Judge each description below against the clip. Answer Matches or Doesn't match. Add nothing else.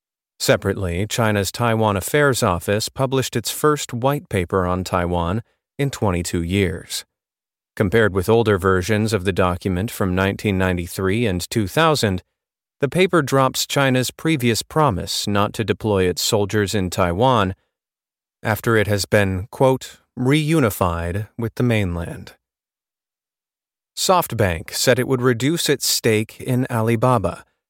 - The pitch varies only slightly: Doesn't match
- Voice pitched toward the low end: Matches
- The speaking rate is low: Matches